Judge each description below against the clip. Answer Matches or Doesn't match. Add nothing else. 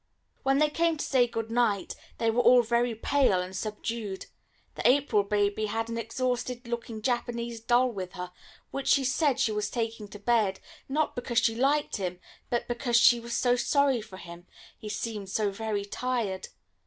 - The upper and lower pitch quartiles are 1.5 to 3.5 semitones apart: Matches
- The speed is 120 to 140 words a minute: Doesn't match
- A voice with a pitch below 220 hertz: Doesn't match